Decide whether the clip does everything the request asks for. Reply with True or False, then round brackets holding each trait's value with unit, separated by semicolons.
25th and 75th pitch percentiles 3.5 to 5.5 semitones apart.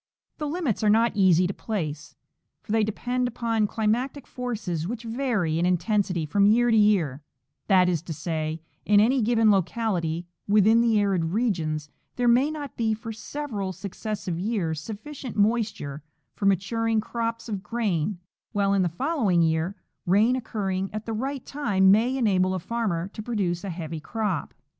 True (4.3 semitones)